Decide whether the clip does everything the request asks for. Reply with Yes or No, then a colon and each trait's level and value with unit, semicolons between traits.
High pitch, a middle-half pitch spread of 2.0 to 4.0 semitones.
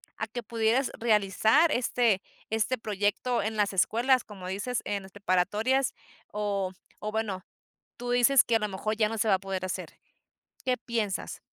Yes: high, 215 Hz; average, 3.2 semitones